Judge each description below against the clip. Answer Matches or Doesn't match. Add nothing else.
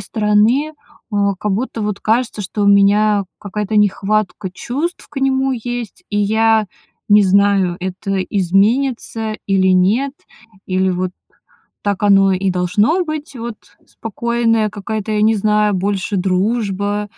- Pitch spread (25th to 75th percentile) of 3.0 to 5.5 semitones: Doesn't match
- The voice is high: Matches